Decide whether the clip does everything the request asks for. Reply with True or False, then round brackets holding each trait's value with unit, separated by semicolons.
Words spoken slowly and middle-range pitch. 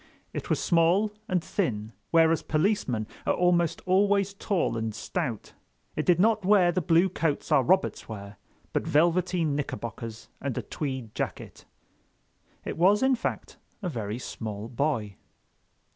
False (145 wpm; 165 Hz)